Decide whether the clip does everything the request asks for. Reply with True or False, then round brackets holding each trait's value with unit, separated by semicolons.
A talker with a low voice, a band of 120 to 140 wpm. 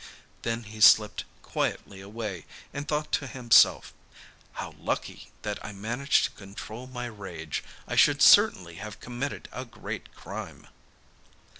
True (110 Hz; 135 wpm)